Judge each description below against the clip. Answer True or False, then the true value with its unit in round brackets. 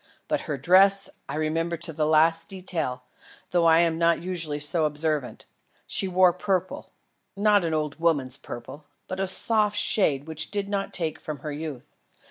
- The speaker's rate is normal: True (170 wpm)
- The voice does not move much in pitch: False (3.6 semitones)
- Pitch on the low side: False (165 Hz)